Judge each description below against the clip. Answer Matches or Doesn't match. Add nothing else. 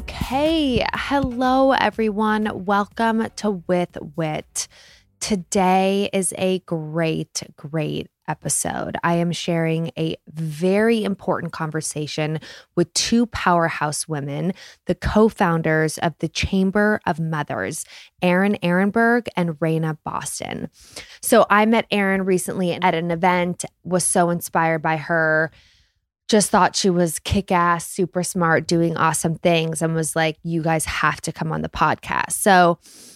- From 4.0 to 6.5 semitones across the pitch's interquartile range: Doesn't match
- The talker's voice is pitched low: Doesn't match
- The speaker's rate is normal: Doesn't match